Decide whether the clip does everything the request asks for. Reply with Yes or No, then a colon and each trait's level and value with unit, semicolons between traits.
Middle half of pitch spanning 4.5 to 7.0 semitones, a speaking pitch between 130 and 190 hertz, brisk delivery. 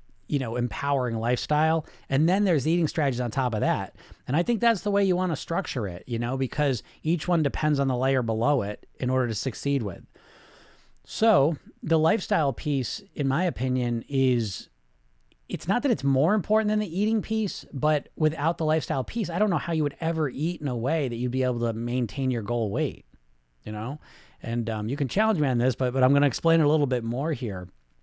Yes: average, 5.1 semitones; medium, 140 Hz; fast, 225 wpm